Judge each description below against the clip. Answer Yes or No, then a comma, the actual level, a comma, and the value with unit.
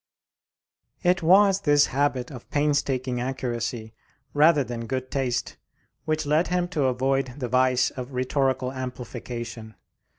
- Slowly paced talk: Yes, slow, 125 wpm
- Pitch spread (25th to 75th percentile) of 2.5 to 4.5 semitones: Yes, average, 2.8 semitones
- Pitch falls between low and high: No, low, 130 Hz